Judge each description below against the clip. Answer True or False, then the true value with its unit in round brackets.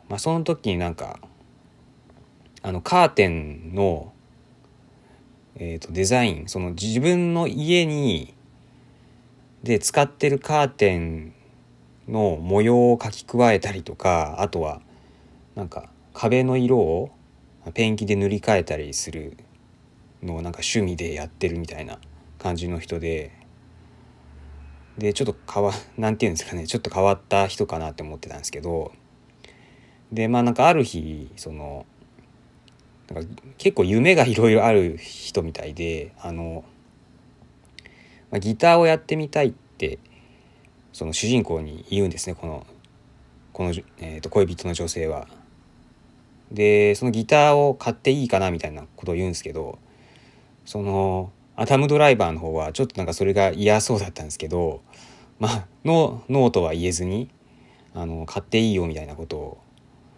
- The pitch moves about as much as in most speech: False (6.9 semitones)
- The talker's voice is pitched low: True (100 Hz)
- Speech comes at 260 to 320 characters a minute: True (275 characters per minute)